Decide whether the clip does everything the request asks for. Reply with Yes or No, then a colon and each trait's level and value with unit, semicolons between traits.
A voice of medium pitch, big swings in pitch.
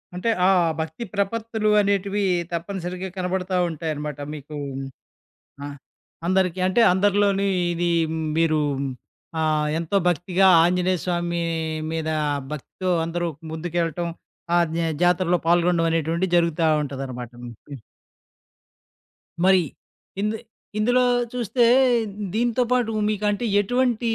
No: medium, 180 Hz; average, 3.5 semitones